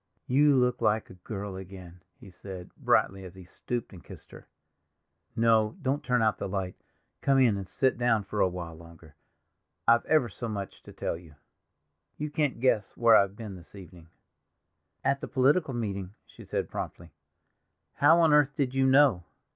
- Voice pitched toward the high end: No, low, 110 Hz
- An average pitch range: No, wide, 5.9 semitones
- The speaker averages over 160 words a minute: Yes, average, 175 wpm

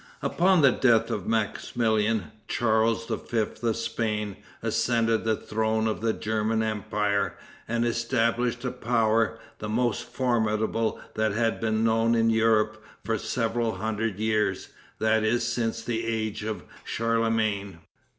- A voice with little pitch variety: Yes, narrow, 1.0 semitones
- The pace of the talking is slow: Yes, slow, 130 wpm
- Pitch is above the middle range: No, low, 110 Hz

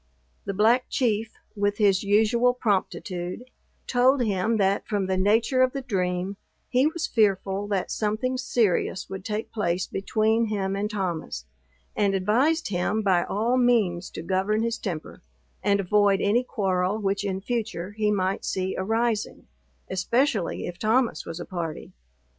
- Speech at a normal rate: Yes, average, 150 wpm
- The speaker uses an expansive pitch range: No, average, 3.3 semitones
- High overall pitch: Yes, high, 205 Hz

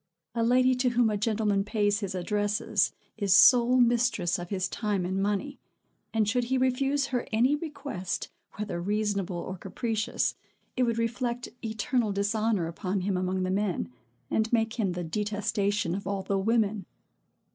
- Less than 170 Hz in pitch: No, high, 210 Hz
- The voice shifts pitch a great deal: No, average, 3.3 semitones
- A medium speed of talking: Yes, average, 160 wpm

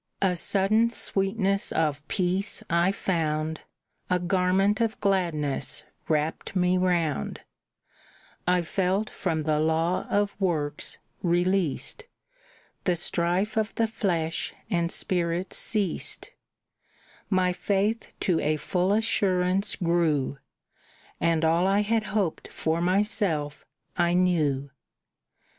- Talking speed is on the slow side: Yes, slow, 110 wpm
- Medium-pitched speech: Yes, medium, 180 Hz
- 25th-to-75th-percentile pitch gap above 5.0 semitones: No, average, 3.3 semitones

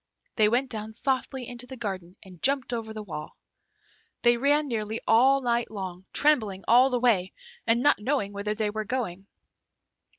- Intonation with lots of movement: No, average, 3.6 semitones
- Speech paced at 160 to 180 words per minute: Yes, average, 170 wpm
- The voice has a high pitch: Yes, high, 230 Hz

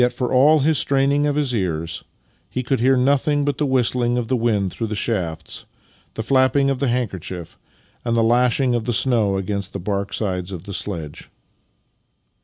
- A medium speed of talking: Yes, average, 185 wpm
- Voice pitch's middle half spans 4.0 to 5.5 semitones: Yes, average, 5.1 semitones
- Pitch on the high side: No, low, 120 Hz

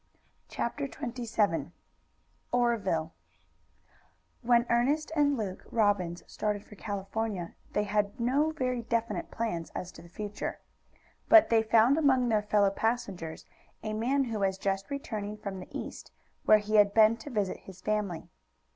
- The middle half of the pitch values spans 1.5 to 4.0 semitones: Yes, average, 3.3 semitones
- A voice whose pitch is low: No, high, 215 Hz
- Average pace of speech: Yes, average, 145 wpm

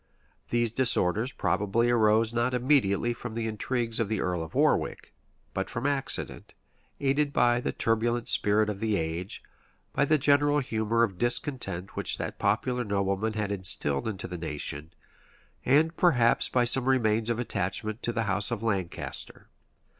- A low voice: Yes, low, 115 Hz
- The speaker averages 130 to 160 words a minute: Yes, average, 155 wpm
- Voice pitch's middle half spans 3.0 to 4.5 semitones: Yes, average, 3.6 semitones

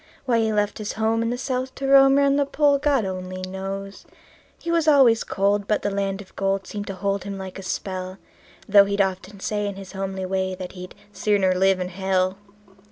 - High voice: Yes, high, 200 Hz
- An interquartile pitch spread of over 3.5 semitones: No, average, 3.0 semitones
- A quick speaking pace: Yes, fast, 215 wpm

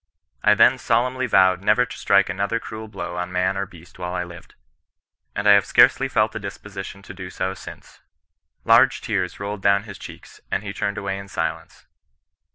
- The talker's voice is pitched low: Yes, low, 100 Hz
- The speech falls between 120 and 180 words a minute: No, average, 190 wpm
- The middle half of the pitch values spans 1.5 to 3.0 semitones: Yes, narrow, 2.5 semitones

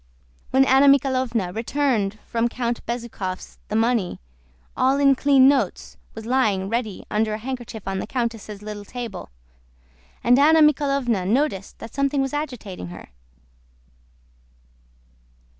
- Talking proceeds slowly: Yes, slow, 125 wpm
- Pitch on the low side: No, high, 240 Hz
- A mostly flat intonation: No, average, 4.1 semitones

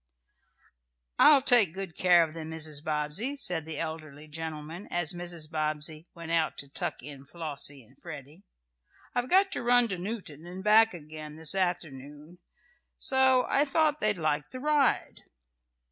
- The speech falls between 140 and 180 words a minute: Yes, average, 155 wpm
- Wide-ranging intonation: Yes, wide, 5.7 semitones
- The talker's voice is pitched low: No, medium, 165 Hz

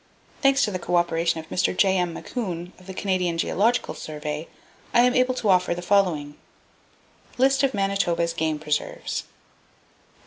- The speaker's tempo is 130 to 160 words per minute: Yes, average, 150 wpm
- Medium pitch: Yes, medium, 180 Hz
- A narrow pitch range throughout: No, average, 3.7 semitones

